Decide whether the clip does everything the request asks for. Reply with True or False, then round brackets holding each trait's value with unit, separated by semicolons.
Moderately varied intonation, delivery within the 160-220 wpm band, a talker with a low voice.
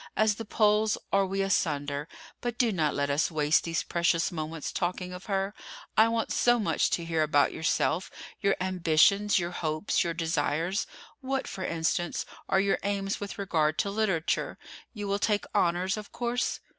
False (4.0 semitones; 170 wpm; 185 Hz)